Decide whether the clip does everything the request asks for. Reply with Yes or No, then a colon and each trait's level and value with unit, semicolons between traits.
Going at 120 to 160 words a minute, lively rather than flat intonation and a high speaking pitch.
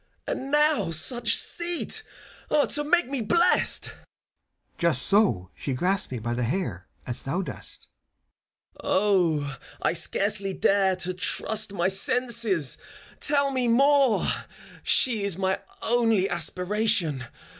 Yes: slow, 135 wpm; wide, 6.1 semitones; high, 200 Hz